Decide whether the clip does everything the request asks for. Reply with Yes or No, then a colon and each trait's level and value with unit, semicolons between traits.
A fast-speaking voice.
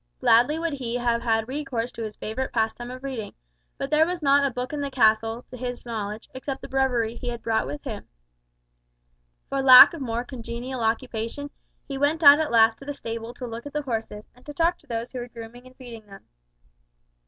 Yes: fast, 215 wpm